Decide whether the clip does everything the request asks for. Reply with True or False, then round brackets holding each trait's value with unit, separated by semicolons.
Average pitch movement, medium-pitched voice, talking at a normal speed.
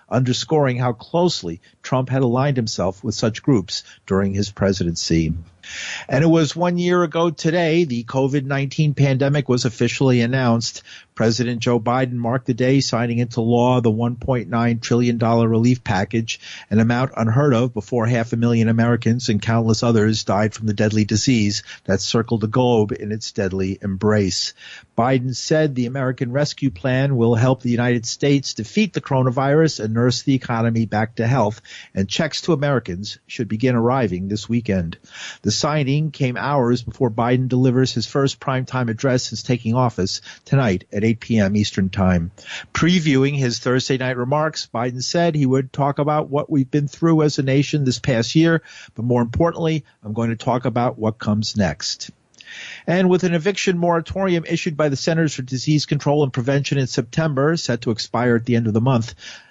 False (3.7 semitones; 125 Hz; 175 wpm)